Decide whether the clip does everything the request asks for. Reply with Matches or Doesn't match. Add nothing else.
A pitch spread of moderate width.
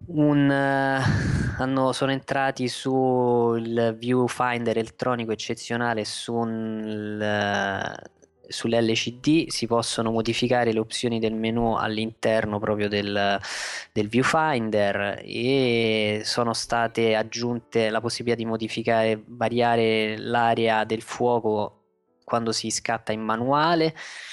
Doesn't match